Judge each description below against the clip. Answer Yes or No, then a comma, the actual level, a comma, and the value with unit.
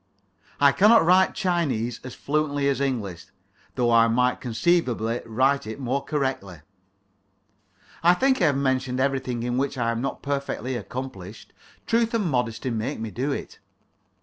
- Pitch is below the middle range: Yes, low, 130 Hz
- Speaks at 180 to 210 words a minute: No, average, 150 wpm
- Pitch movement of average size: Yes, average, 3.6 semitones